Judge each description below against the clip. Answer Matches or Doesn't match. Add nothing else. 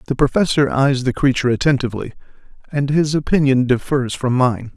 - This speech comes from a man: Matches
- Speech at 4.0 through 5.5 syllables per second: Doesn't match